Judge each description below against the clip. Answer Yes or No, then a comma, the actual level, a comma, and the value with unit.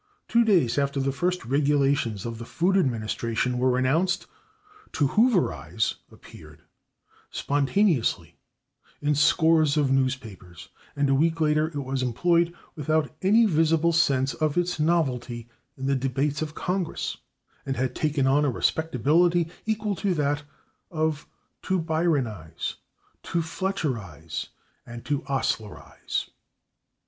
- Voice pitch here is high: No, medium, 145 Hz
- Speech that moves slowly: Yes, slow, 125 wpm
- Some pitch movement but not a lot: Yes, average, 4.3 semitones